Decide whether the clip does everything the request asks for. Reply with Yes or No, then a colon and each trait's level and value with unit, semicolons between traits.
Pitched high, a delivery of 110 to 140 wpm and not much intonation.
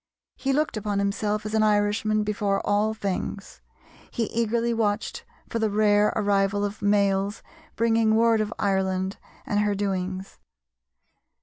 Yes: high, 210 Hz; slow, 135 wpm; narrow, 1.5 semitones